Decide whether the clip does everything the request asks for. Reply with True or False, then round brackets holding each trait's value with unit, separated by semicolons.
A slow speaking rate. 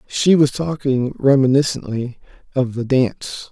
True (120 wpm)